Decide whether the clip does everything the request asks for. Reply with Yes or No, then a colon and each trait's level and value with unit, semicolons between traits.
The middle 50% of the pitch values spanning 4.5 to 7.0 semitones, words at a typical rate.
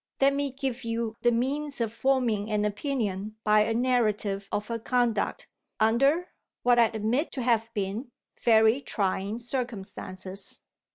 No: average, 3.2 semitones; average, 145 wpm